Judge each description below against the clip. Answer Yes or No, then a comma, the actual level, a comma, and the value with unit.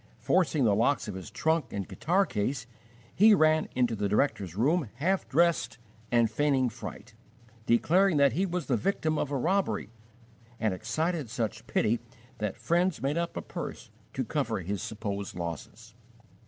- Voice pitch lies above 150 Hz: No, low, 130 Hz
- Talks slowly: No, average, 160 wpm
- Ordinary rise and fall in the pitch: No, wide, 7.4 semitones